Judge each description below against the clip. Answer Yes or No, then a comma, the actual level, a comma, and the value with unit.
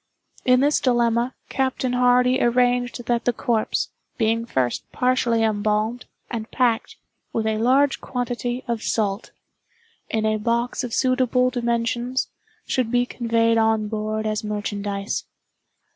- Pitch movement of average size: No, narrow, 2.2 semitones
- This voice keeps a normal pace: No, slow, 130 wpm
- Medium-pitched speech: No, high, 235 Hz